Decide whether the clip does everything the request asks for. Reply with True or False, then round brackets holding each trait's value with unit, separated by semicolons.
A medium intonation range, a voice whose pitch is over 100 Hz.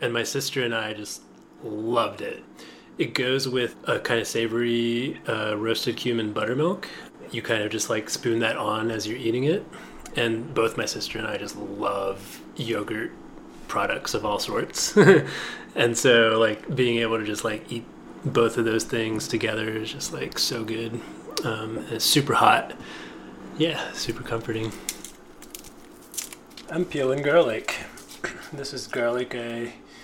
False (1.2 semitones; 115 Hz)